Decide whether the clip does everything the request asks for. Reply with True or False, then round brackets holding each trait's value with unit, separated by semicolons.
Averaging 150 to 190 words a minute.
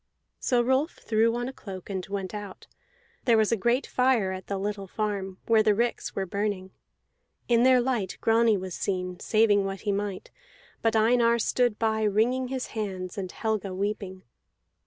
True (175 wpm)